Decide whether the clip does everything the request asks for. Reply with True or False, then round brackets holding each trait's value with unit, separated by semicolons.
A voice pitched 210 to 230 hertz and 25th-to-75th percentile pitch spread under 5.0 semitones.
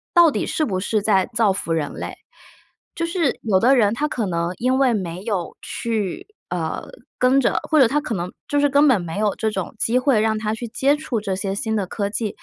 False (220 Hz; 5.4 semitones)